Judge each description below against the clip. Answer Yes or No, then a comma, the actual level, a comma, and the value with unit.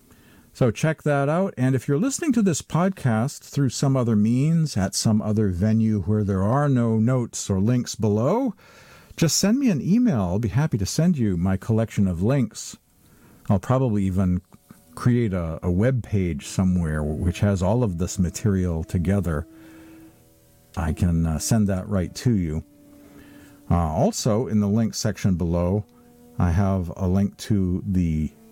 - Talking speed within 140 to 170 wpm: Yes, average, 165 wpm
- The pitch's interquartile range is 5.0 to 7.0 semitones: Yes, wide, 5.6 semitones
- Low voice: Yes, low, 105 Hz